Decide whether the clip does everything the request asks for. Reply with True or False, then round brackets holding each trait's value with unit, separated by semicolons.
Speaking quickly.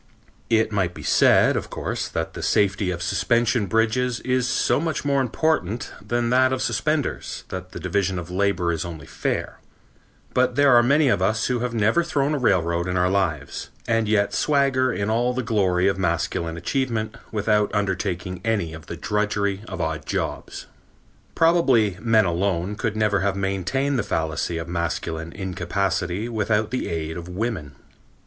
False (170 wpm)